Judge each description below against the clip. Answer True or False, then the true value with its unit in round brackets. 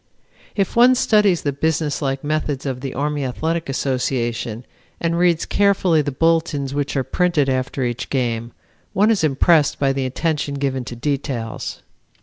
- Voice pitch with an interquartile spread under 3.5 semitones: False (3.9 semitones)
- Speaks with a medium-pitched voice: True (145 Hz)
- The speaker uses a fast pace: False (150 wpm)